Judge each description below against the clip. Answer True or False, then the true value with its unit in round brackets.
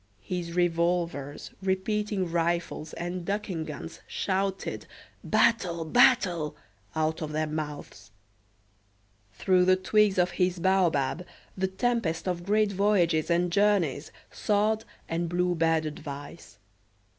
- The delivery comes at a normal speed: False (110 wpm)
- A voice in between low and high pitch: True (175 Hz)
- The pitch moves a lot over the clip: False (2.9 semitones)